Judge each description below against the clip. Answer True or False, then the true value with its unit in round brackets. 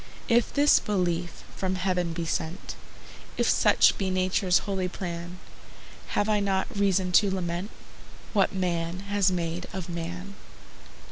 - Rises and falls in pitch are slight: True (2.1 semitones)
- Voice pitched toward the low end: False (185 Hz)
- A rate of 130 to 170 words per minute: True (135 wpm)